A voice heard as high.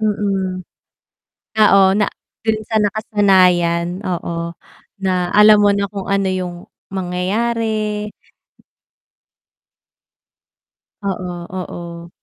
Yes: high, 195 Hz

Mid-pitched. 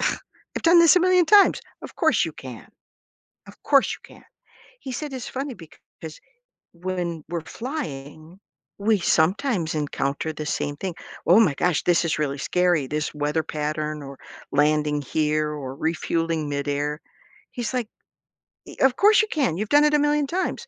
Yes: medium, 165 Hz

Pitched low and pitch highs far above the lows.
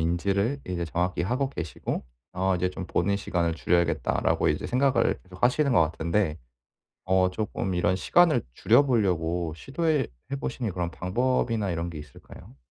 Yes: very low, 95 Hz; wide, 5.8 semitones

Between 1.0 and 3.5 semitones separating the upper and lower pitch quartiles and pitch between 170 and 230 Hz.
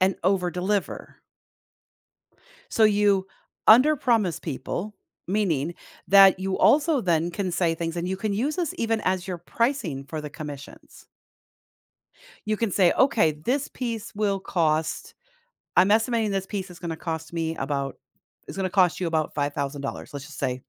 No: average, 4.6 semitones; medium, 185 Hz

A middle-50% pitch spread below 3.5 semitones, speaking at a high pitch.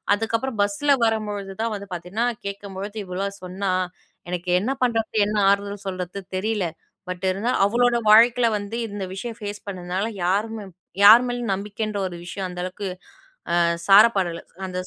Yes: average, 2.8 semitones; high, 200 Hz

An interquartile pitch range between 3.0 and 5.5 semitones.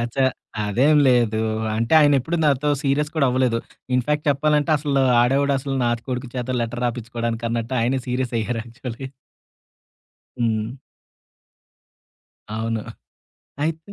Yes: average, 3.3 semitones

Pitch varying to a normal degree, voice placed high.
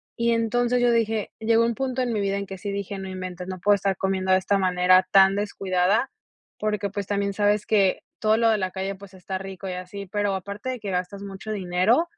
No: narrow, 2.3 semitones; high, 200 Hz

